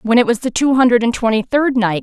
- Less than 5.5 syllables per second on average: No, 6.0 syllables/s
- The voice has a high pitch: Yes, high, 240 Hz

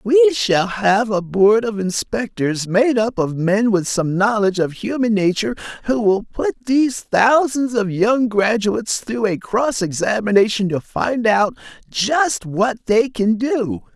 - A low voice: No, high, 215 Hz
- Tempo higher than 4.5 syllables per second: No, 4.0 syllables/s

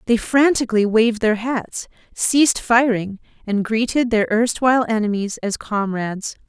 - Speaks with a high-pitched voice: Yes, high, 225 Hz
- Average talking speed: No, slow, 130 wpm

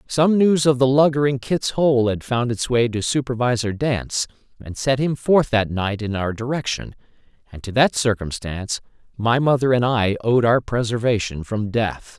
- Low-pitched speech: Yes, low, 120 Hz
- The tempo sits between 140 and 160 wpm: No, average, 180 wpm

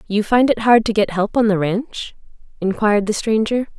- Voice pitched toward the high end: Yes, high, 215 Hz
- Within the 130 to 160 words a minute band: No, fast, 205 wpm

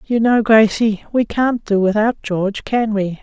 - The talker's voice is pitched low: No, high, 215 Hz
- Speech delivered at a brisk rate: No, average, 185 wpm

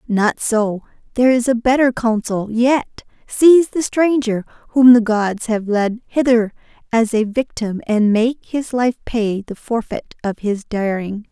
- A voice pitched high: Yes, high, 230 Hz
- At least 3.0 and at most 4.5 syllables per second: Yes, 4.1 syllables/s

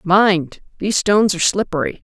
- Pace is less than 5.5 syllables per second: No, 5.7 syllables/s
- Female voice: Yes, female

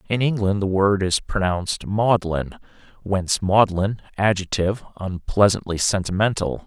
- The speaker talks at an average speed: No, slow, 110 wpm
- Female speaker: No, male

